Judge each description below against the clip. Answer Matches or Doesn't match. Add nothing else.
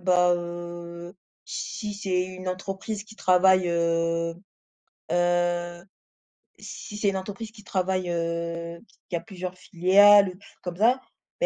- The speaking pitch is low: Doesn't match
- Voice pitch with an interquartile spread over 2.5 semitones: Doesn't match